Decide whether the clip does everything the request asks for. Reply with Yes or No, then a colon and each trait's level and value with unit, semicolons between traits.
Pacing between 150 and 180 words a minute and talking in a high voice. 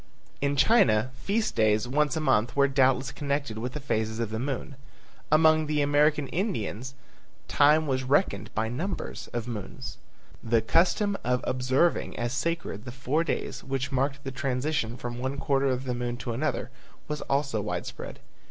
No: average, 165 wpm; low, 135 Hz